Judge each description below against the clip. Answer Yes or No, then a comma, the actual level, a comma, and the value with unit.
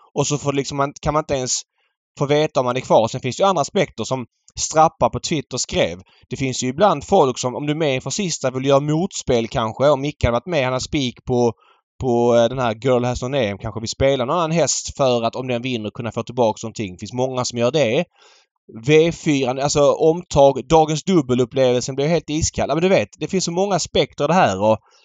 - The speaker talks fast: Yes, fast, 230 wpm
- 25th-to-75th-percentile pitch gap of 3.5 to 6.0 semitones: Yes, average, 4.0 semitones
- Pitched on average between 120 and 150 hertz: Yes, low, 130 Hz